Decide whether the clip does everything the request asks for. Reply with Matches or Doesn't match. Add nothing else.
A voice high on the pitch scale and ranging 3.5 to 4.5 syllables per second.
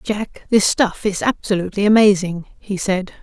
Doesn't match